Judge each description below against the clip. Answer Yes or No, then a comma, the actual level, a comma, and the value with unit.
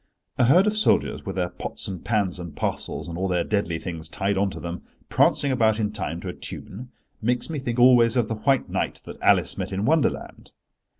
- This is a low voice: Yes, low, 105 Hz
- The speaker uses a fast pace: Yes, fast, 220 wpm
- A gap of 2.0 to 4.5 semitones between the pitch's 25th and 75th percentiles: No, average, 5.1 semitones